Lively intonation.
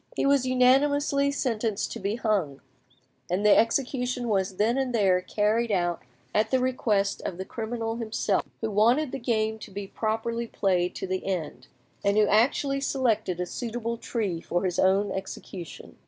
No: average, 4.2 semitones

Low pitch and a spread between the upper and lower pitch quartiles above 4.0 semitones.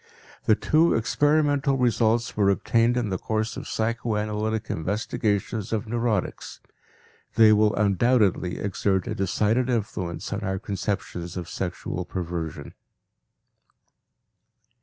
No: low, 105 Hz; average, 3.3 semitones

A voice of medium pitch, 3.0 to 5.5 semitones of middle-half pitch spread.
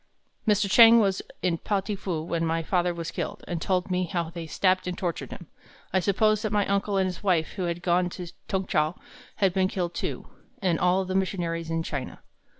No: medium, 180 Hz; narrow, 2.4 semitones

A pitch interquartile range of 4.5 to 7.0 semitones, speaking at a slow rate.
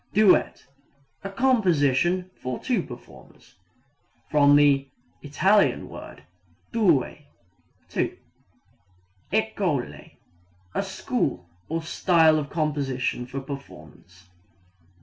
Yes: wide, 5.5 semitones; slow, 85 wpm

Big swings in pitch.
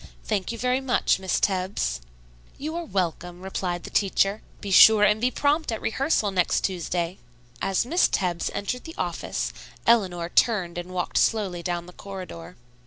No: average, 4.5 semitones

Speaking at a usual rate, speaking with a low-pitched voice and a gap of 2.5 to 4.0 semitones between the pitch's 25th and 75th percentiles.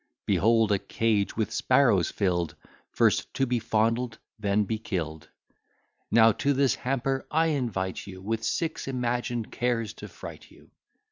Yes: average, 145 wpm; low, 115 Hz; average, 3.4 semitones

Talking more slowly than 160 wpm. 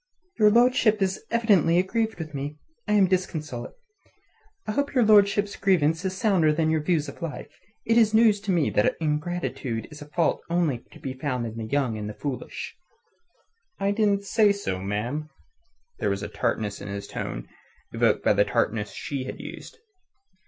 No: average, 180 wpm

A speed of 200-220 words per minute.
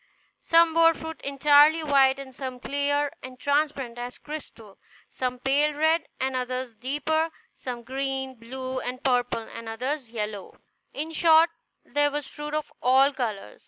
No: average, 150 wpm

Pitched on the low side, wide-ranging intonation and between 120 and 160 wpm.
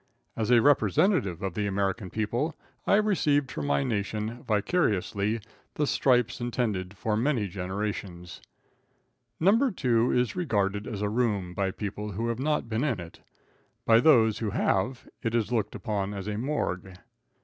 No: low, 110 Hz; average, 3.8 semitones; average, 155 wpm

